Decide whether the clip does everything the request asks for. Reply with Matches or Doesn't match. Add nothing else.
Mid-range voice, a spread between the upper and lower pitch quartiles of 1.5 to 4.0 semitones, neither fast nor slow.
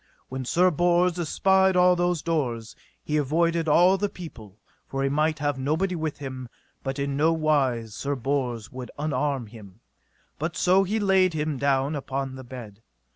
Doesn't match